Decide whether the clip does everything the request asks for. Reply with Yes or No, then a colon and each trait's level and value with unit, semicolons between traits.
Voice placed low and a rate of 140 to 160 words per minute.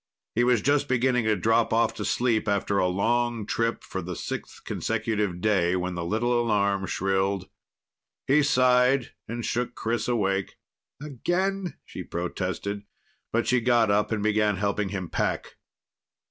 Yes: low, 110 Hz; average, 150 wpm